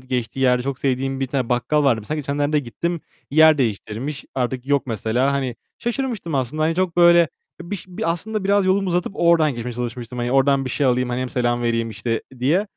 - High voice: No, low, 135 Hz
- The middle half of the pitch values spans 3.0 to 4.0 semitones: No, average, 5.1 semitones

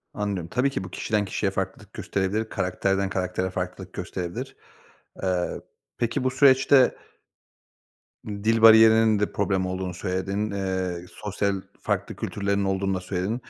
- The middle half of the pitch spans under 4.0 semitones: Yes, average, 2.8 semitones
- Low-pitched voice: Yes, low, 100 Hz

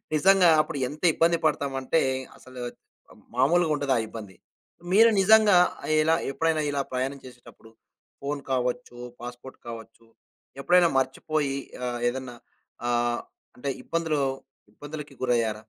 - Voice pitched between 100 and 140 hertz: Yes, low, 135 Hz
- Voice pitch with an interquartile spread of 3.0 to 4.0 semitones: No, average, 4.7 semitones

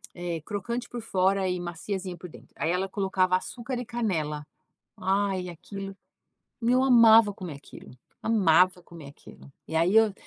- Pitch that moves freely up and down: No, average, 3.8 semitones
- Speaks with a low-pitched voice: No, high, 190 Hz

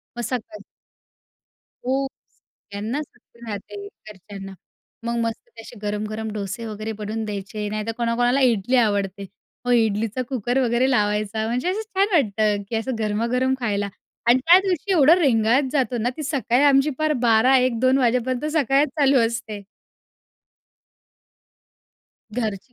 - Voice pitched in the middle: No, high, 235 Hz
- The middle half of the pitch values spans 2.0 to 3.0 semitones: No, average, 3.7 semitones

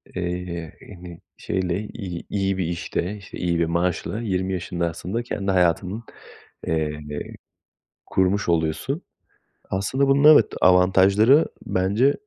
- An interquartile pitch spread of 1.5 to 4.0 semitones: Yes, average, 2.9 semitones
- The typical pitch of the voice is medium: No, very low, 95 Hz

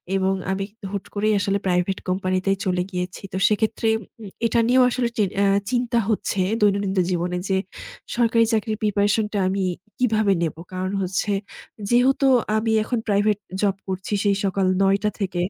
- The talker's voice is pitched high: Yes, high, 200 Hz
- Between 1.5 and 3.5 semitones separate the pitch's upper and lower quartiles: Yes, narrow, 2.5 semitones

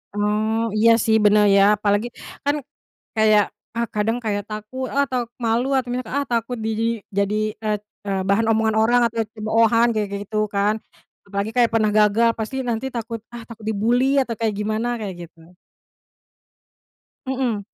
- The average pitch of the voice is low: No, high, 220 Hz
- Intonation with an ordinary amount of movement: No, narrow, 1.9 semitones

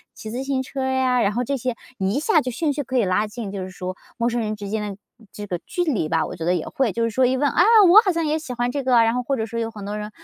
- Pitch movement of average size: Yes, average, 4.1 semitones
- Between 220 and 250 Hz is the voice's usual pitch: Yes, high, 240 Hz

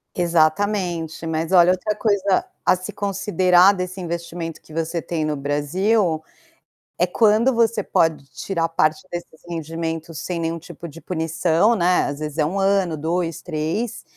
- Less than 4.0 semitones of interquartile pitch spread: Yes, average, 2.7 semitones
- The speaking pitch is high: No, medium, 170 Hz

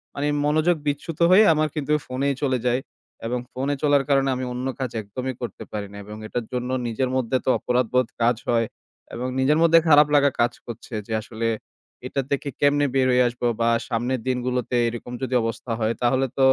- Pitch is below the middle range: Yes, low, 130 Hz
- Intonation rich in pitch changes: No, average, 2.8 semitones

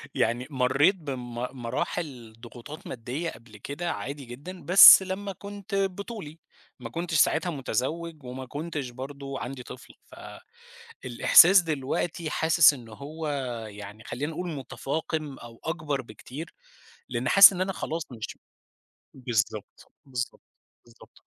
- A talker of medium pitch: Yes, medium, 145 Hz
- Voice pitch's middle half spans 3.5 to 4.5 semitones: No, average, 5.3 semitones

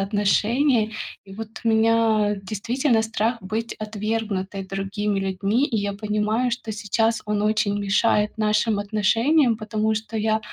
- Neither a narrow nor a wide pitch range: No, narrow, 1.7 semitones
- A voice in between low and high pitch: No, high, 215 Hz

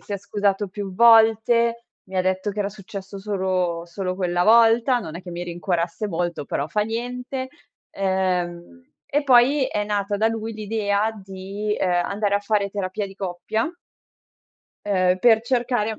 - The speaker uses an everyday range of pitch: Yes, average, 3.2 semitones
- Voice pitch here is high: Yes, high, 200 Hz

